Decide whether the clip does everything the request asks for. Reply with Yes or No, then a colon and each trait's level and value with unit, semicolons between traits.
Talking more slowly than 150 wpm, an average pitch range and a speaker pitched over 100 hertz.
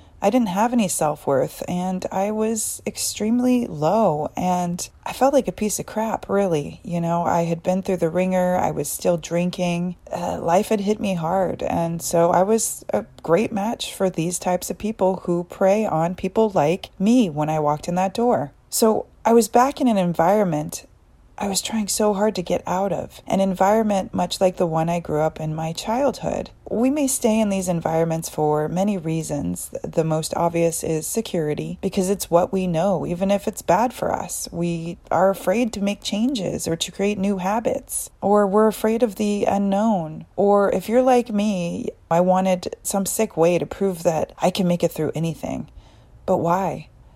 No: average, 195 wpm; average, 3.9 semitones; high, 190 Hz